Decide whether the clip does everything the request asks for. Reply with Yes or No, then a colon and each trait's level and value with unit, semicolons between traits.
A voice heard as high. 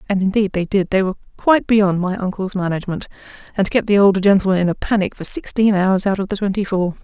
Yes: high, 195 Hz